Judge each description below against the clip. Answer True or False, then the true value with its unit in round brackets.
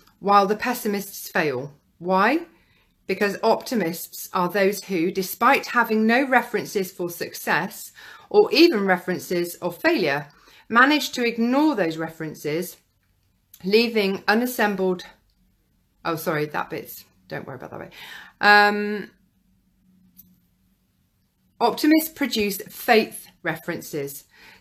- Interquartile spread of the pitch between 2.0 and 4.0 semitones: False (4.7 semitones)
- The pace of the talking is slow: True (100 wpm)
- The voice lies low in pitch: False (195 Hz)